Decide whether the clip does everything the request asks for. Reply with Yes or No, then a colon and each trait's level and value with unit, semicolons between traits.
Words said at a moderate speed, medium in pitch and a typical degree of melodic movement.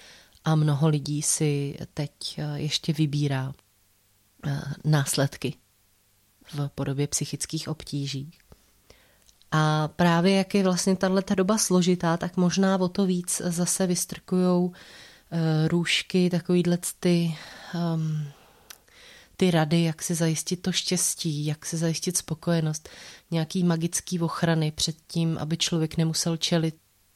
No: slow, 110 wpm; medium, 165 Hz; average, 3.2 semitones